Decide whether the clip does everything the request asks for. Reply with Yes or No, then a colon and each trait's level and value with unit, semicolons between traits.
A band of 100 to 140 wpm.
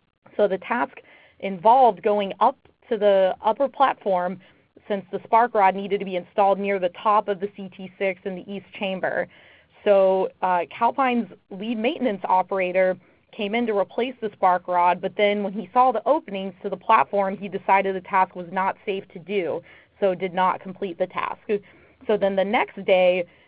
No: average, 180 wpm